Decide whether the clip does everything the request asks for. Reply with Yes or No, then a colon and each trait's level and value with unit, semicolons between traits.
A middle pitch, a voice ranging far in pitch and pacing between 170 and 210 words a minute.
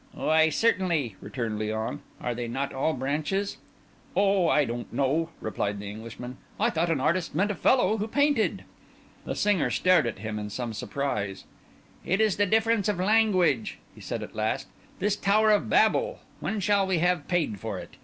Yes: medium, 165 Hz; wide, 8.9 semitones; average, 180 wpm